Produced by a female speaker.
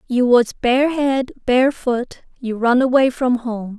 Yes: female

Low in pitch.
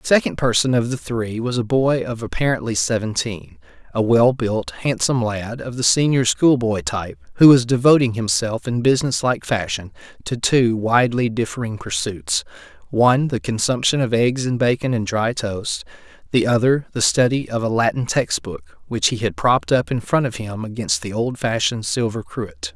Yes: low, 115 Hz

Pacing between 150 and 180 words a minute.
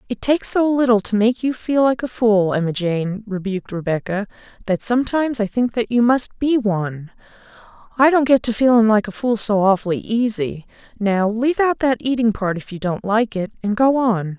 No: fast, 205 wpm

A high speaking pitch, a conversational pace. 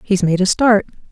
No: high, 200 Hz; fast, 215 wpm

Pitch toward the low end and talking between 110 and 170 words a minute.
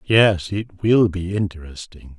Yes: very low, 95 Hz; slow, 135 wpm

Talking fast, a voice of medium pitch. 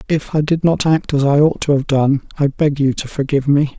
Yes: fast, 270 wpm; medium, 145 Hz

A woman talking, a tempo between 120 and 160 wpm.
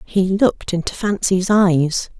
Yes: female; slow, 135 wpm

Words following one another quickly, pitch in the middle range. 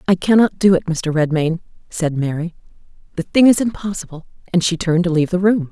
Yes: fast, 210 wpm; medium, 175 Hz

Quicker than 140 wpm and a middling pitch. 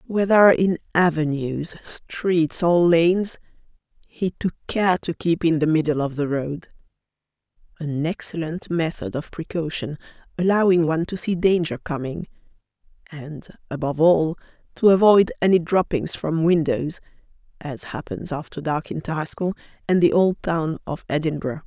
No: slow, 135 wpm; medium, 165 Hz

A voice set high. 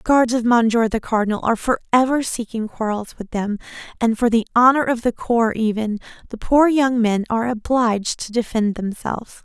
Yes: high, 230 Hz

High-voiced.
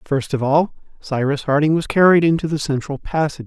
No: medium, 150 Hz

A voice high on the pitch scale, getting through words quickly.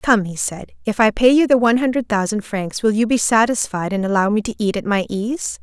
Yes: high, 220 Hz; fast, 255 wpm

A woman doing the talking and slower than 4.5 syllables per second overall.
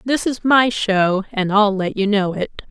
Yes: female; 4.1 syllables/s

